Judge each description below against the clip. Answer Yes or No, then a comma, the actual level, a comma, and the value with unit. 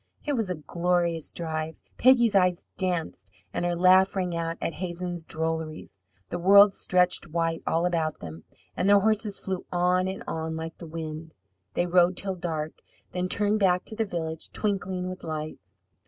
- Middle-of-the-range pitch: Yes, medium, 175 Hz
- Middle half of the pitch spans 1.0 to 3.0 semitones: Yes, narrow, 2.6 semitones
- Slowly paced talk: No, average, 170 wpm